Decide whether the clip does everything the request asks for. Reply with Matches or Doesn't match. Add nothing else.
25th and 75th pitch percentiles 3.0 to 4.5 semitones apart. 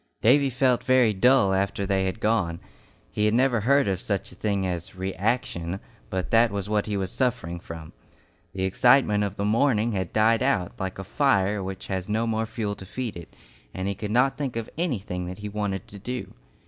Matches